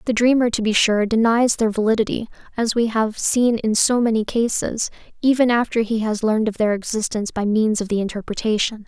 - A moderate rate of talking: Yes, average, 195 wpm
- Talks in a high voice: Yes, high, 220 Hz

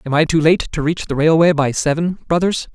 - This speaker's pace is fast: Yes, fast, 240 wpm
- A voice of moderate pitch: Yes, medium, 160 Hz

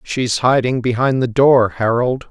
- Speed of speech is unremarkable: Yes, average, 155 wpm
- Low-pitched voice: Yes, low, 125 Hz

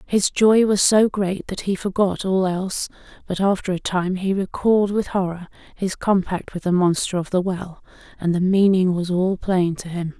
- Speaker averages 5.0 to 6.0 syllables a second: No, 4.8 syllables/s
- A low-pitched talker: No, high, 190 Hz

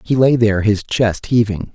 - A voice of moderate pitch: No, low, 110 Hz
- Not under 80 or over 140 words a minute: No, fast, 205 wpm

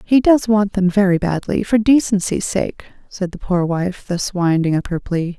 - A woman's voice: Yes, female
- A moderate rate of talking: Yes, average, 190 wpm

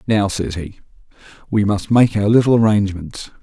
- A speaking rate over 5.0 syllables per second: Yes, 5.2 syllables/s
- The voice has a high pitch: No, low, 100 Hz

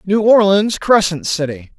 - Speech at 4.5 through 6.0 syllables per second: No, 4.3 syllables/s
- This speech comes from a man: Yes, male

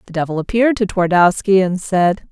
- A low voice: No, high, 190 Hz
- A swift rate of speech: No, average, 180 wpm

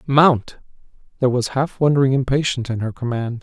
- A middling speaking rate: Yes, average, 160 wpm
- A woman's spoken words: No, male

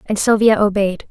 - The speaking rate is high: No, average, 165 wpm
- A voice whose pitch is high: Yes, high, 205 Hz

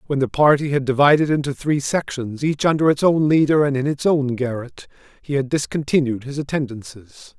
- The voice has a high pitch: No, medium, 140 Hz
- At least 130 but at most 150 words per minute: No, average, 185 wpm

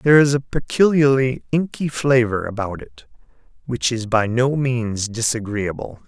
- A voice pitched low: Yes, low, 125 Hz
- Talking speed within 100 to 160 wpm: Yes, average, 140 wpm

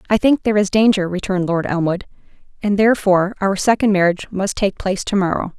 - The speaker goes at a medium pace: Yes, average, 195 wpm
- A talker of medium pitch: No, high, 195 Hz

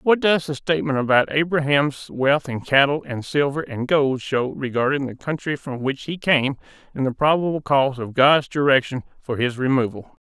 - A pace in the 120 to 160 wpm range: No, average, 180 wpm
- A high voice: No, medium, 140 Hz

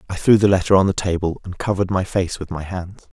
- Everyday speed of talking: No, fast, 265 wpm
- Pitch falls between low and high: No, very low, 95 Hz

